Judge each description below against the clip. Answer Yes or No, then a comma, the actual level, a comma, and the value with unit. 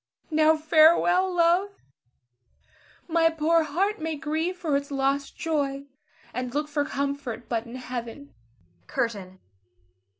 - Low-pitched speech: No, very high, 300 Hz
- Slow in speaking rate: Yes, slow, 120 wpm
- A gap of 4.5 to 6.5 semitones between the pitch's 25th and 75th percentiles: No, average, 3.2 semitones